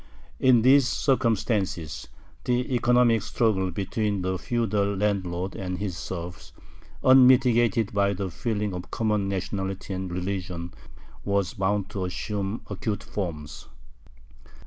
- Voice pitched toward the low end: Yes, low, 100 Hz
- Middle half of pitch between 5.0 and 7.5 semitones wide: No, average, 3.6 semitones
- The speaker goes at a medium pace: No, slow, 115 wpm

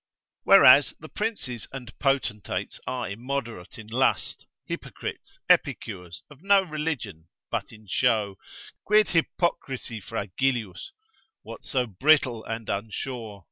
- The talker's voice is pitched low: Yes, low, 120 Hz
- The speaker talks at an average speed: No, slow, 110 wpm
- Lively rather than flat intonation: No, average, 4.7 semitones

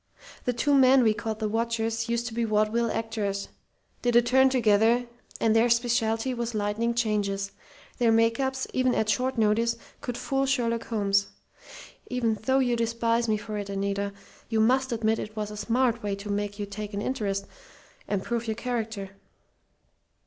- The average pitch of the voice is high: Yes, high, 225 Hz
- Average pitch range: No, narrow, 2.2 semitones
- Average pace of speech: Yes, average, 175 wpm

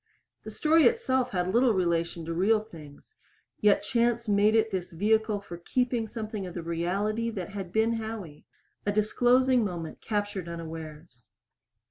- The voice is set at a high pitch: Yes, high, 205 Hz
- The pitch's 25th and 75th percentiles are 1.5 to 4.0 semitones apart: No, average, 4.7 semitones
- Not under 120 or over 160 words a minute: Yes, average, 150 wpm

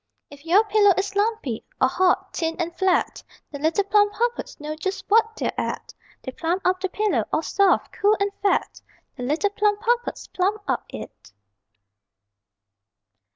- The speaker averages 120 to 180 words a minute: Yes, average, 155 wpm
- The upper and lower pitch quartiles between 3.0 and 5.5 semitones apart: Yes, average, 3.9 semitones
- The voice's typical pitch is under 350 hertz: No, very high, 390 Hz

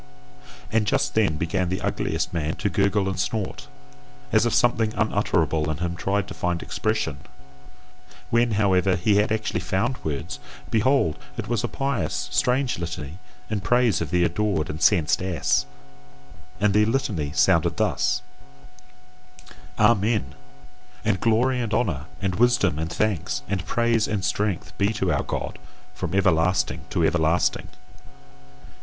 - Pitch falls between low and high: No, low, 100 Hz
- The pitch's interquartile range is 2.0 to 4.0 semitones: No, average, 4.4 semitones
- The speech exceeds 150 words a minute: No, average, 145 wpm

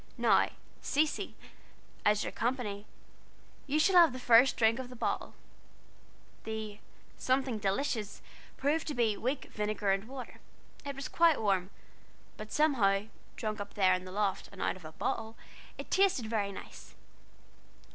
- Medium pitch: No, high, 220 Hz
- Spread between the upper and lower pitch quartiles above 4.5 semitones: Yes, average, 4.9 semitones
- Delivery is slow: No, average, 155 wpm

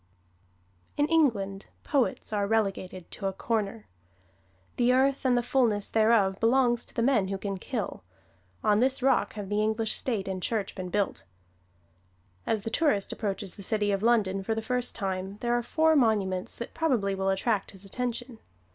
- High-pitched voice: Yes, high, 220 Hz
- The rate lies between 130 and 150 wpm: No, average, 175 wpm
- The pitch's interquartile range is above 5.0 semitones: No, average, 3.7 semitones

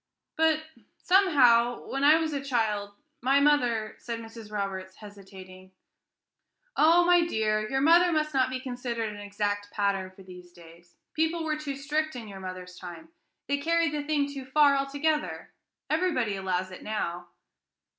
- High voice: Yes, high, 245 Hz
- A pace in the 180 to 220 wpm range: No, average, 155 wpm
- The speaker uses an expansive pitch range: Yes, wide, 7.1 semitones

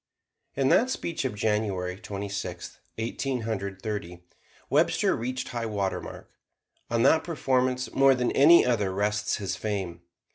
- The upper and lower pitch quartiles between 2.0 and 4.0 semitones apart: No, average, 4.5 semitones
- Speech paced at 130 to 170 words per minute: Yes, average, 145 wpm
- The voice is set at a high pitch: No, low, 110 Hz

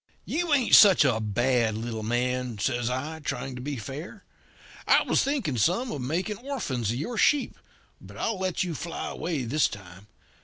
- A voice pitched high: No, low, 135 Hz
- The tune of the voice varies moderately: No, wide, 7.8 semitones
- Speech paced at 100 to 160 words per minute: No, average, 180 wpm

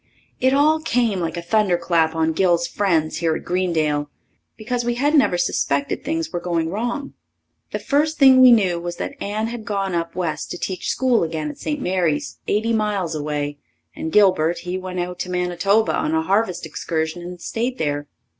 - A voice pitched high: No, medium, 180 Hz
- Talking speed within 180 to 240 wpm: Yes, average, 185 wpm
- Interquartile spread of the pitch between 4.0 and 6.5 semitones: Yes, average, 5.3 semitones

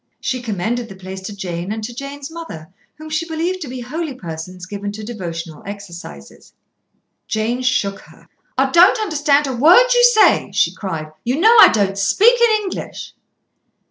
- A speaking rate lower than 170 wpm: No, average, 175 wpm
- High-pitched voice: Yes, high, 240 Hz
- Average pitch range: No, wide, 8.6 semitones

